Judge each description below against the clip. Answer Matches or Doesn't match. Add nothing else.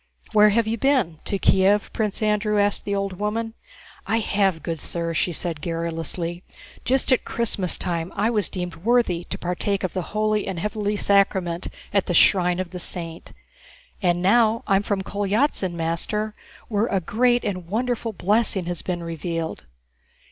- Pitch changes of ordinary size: Matches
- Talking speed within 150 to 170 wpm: Matches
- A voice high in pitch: Matches